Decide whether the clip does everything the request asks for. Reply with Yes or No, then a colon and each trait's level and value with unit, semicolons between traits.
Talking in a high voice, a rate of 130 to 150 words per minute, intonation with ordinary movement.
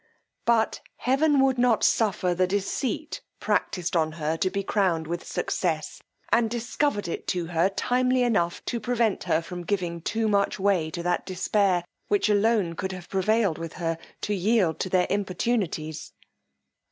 No: high, 195 Hz; average, 160 wpm; average, 4.5 semitones